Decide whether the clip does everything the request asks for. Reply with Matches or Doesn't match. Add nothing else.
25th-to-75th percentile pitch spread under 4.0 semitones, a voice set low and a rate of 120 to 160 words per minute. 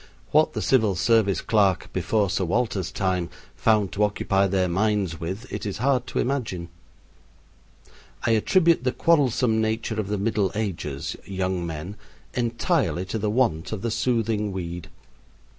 Matches